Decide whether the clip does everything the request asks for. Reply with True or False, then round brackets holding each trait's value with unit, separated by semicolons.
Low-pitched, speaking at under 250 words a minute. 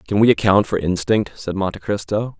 True (100 Hz; 200 wpm)